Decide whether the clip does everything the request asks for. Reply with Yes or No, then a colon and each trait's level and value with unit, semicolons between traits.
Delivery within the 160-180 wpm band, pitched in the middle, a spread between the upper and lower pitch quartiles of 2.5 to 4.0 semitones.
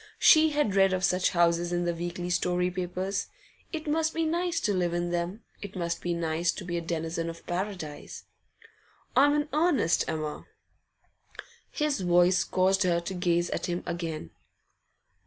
Yes: average, 165 wpm; medium, 180 Hz; average, 2.8 semitones